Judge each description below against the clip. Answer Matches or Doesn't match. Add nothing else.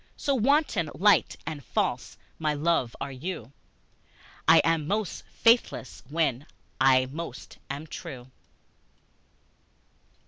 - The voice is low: Doesn't match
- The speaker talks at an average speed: Doesn't match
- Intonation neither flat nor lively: Matches